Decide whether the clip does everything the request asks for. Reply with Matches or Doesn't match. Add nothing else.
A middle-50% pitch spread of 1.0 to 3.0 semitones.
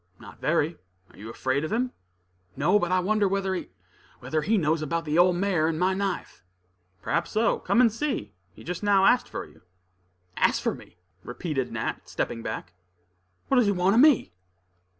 Doesn't match